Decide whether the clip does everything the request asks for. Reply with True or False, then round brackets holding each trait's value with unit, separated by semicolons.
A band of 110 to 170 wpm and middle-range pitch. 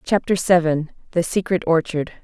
True (135 wpm; 170 Hz)